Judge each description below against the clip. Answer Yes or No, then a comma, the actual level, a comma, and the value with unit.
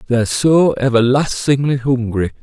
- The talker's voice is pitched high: No, low, 125 Hz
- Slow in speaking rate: Yes, slow, 100 wpm